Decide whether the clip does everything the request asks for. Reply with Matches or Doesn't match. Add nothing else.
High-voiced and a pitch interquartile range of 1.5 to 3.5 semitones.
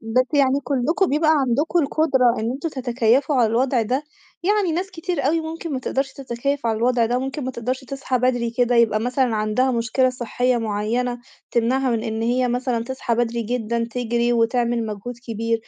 Matches